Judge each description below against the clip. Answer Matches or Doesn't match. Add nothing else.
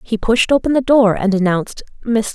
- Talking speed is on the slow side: Doesn't match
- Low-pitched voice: Doesn't match